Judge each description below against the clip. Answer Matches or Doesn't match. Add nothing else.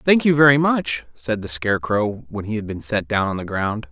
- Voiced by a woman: Doesn't match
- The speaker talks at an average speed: Doesn't match